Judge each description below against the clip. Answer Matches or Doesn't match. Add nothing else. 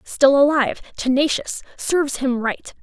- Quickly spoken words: Doesn't match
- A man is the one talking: Doesn't match